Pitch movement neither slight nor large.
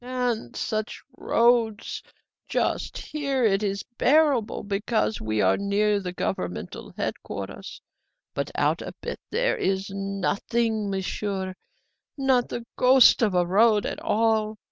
Yes: average, 3.4 semitones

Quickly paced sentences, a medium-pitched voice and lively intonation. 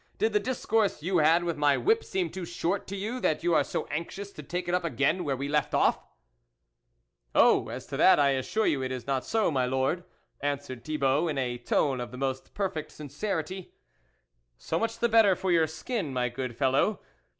Yes: fast, 215 wpm; medium, 150 Hz; wide, 6.1 semitones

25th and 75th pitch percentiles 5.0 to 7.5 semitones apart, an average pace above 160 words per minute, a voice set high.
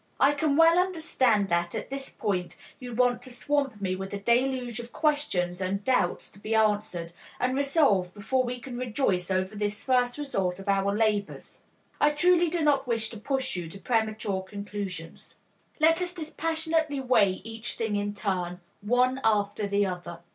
Yes: wide, 5.4 semitones; average, 175 wpm; high, 225 Hz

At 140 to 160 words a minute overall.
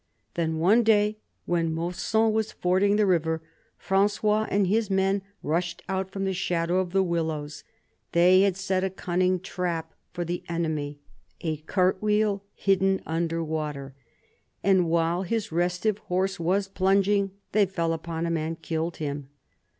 Yes: average, 150 wpm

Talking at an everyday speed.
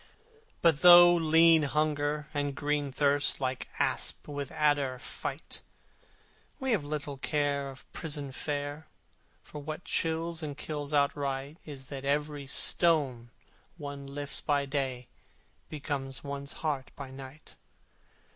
No: slow, 125 wpm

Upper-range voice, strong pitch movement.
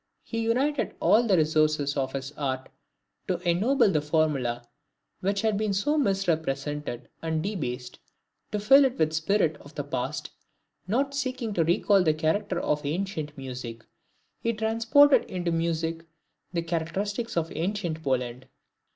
No: medium, 165 Hz; wide, 6.0 semitones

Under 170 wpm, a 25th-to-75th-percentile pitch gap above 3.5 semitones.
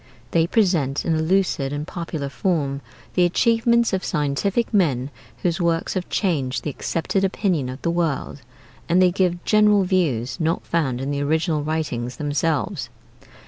Yes: average, 155 wpm; average, 4.6 semitones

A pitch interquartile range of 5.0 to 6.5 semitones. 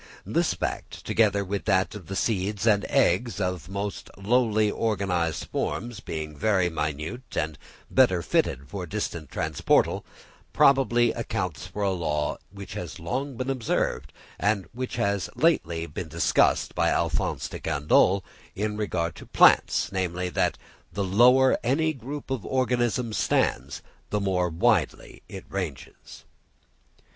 Yes: average, 5.3 semitones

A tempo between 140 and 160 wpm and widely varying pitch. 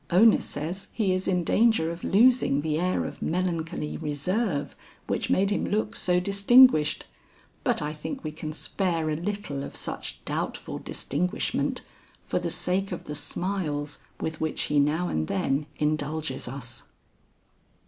No: average, 150 wpm; average, 4.5 semitones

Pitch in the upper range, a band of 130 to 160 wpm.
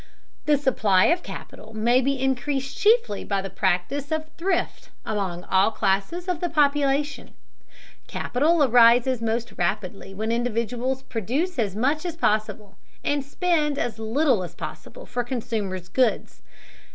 Yes: high, 245 Hz; average, 140 wpm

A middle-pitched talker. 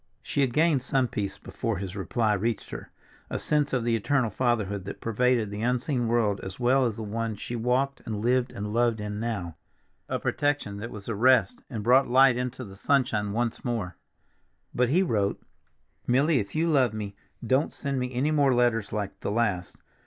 No: low, 120 Hz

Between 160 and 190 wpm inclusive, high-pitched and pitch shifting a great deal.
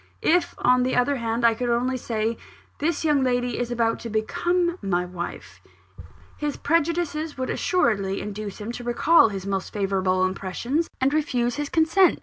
Yes: average, 165 wpm; high, 245 Hz; wide, 5.8 semitones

